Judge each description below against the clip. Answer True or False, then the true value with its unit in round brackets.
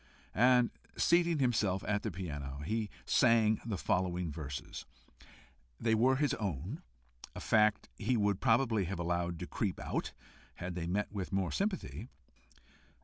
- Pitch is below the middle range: True (105 Hz)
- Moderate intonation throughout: True (4.8 semitones)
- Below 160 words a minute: True (145 wpm)